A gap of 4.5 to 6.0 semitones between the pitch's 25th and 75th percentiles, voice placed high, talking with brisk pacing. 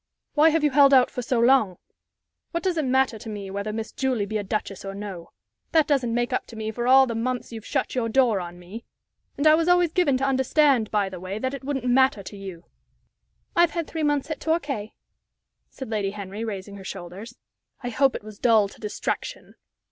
Yes: average, 5.0 semitones; high, 240 Hz; fast, 215 wpm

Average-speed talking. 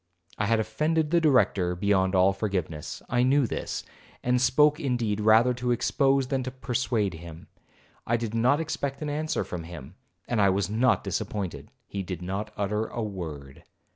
Yes: average, 170 wpm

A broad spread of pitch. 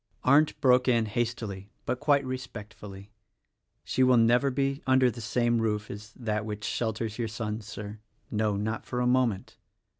No: average, 3.1 semitones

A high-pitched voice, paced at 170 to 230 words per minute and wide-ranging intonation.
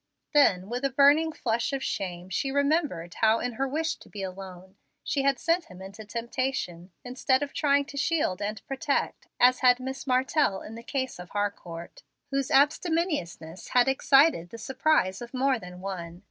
Yes: very high, 250 Hz; average, 175 wpm; wide, 6.5 semitones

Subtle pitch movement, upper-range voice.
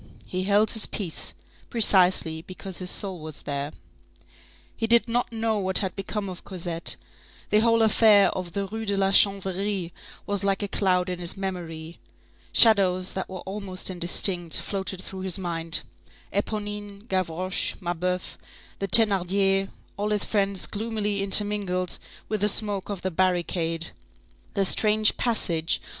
Yes: narrow, 2.3 semitones; high, 195 Hz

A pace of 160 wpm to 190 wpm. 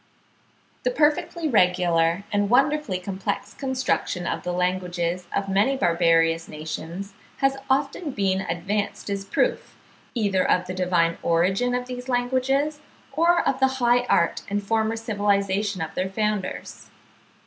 No: slow, 135 wpm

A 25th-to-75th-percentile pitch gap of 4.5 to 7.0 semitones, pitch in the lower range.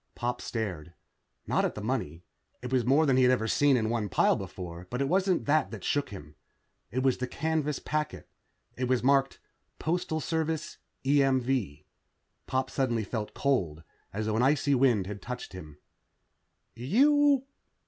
Yes: average, 4.9 semitones; low, 130 Hz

